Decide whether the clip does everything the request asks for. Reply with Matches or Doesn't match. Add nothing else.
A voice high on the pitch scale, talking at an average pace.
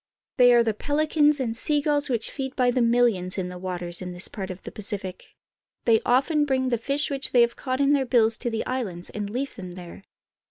Doesn't match